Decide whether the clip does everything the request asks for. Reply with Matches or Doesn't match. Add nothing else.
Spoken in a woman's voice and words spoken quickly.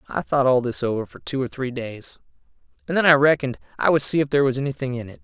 Doesn't match